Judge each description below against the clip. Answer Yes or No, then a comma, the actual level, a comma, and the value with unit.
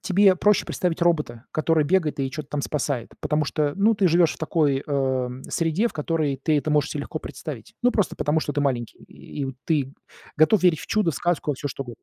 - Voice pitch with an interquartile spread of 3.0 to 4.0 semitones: Yes, average, 3.3 semitones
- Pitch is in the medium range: Yes, medium, 155 Hz